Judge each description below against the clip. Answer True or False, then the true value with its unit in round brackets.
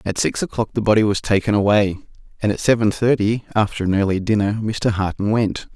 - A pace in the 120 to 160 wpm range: False (200 wpm)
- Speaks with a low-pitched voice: True (105 Hz)